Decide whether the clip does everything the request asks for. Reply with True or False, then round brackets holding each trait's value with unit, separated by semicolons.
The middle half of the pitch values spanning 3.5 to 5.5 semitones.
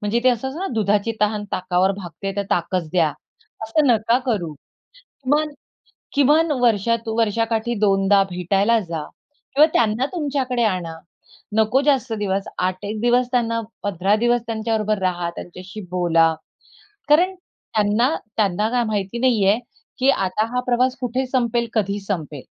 True (3.8 semitones)